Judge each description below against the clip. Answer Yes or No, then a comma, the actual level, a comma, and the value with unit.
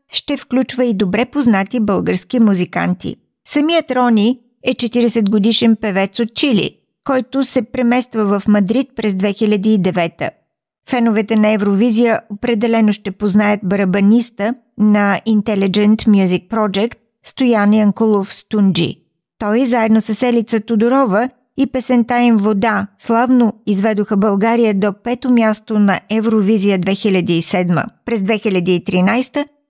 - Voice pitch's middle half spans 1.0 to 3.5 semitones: Yes, average, 2.8 semitones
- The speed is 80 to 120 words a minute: Yes, slow, 115 wpm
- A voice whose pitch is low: No, high, 220 Hz